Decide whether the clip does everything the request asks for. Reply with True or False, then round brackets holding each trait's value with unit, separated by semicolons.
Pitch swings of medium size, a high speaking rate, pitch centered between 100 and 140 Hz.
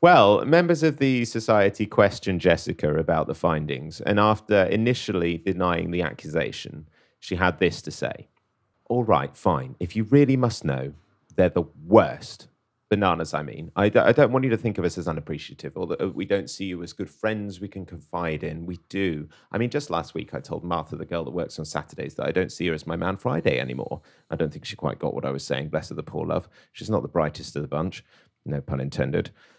False (4.8 semitones; 225 wpm; 90 Hz)